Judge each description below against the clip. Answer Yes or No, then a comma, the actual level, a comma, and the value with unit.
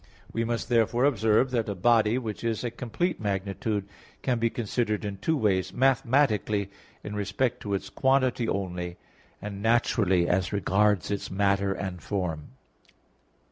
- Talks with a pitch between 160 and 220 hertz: No, low, 105 Hz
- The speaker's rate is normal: Yes, average, 145 wpm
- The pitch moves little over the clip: No, average, 3.3 semitones